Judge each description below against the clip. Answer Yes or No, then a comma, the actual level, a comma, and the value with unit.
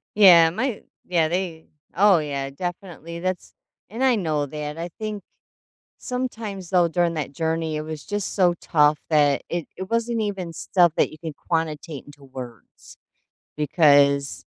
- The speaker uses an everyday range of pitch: Yes, average, 4.0 semitones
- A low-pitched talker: No, medium, 165 Hz